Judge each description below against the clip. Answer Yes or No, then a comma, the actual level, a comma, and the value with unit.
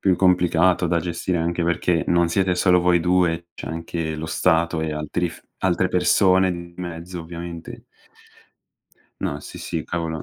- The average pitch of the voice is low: Yes, very low, 85 Hz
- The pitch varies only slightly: Yes, narrow, 1.5 semitones